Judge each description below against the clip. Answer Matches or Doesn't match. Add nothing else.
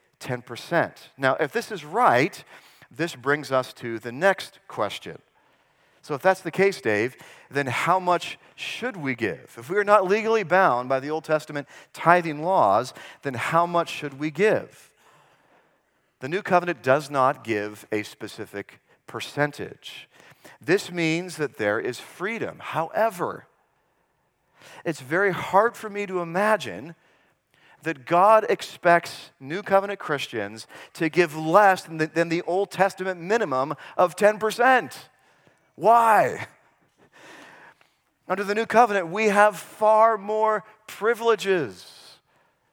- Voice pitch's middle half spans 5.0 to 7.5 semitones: Matches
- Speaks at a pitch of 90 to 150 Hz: Doesn't match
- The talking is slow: Matches